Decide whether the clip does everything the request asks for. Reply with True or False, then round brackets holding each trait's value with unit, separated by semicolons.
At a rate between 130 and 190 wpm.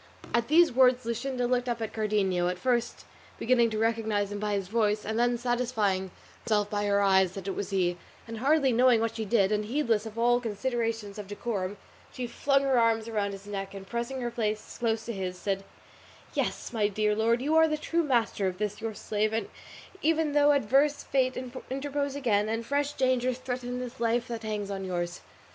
False (200 wpm)